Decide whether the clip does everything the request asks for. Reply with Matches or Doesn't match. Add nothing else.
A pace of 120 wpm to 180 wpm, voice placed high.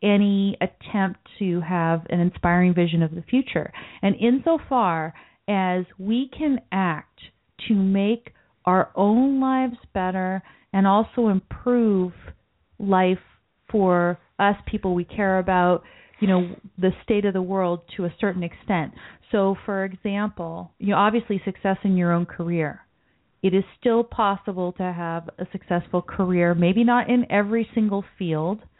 Matches